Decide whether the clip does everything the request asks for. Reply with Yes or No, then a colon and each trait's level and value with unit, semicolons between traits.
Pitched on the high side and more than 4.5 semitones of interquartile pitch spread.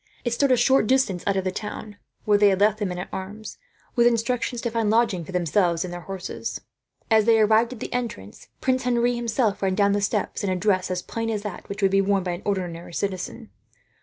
No: high, 205 Hz; average, 3.5 semitones